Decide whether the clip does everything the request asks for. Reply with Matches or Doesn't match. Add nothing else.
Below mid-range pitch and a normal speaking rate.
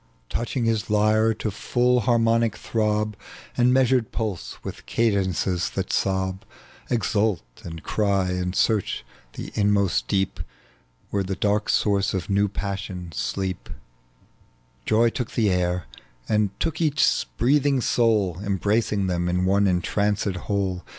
Doesn't match